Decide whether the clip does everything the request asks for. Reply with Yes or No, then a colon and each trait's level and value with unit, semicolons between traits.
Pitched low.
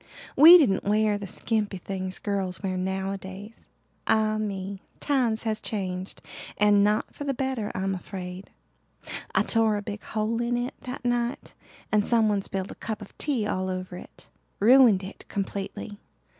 No: high, 210 Hz